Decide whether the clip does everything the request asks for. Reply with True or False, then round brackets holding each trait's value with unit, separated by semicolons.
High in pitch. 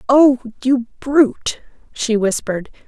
True (245 Hz)